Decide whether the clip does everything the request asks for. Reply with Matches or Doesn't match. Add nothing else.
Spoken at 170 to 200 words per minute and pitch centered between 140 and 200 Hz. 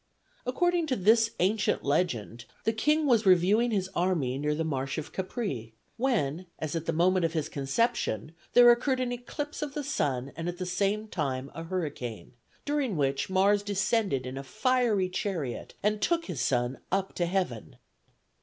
Matches